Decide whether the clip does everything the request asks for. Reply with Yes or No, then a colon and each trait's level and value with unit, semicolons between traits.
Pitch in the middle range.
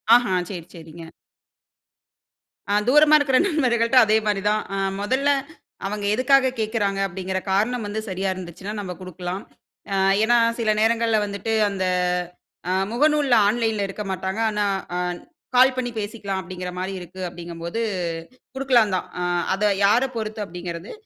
No: high, 210 Hz